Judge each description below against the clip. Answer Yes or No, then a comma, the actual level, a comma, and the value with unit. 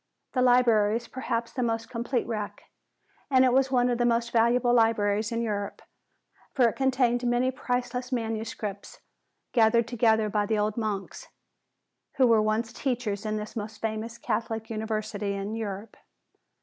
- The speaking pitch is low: No, high, 230 Hz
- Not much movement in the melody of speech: Yes, narrow, 2.2 semitones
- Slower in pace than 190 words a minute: Yes, average, 155 wpm